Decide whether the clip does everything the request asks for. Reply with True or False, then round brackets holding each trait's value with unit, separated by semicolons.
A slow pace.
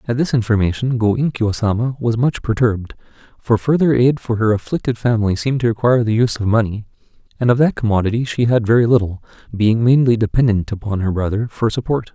False (195 wpm)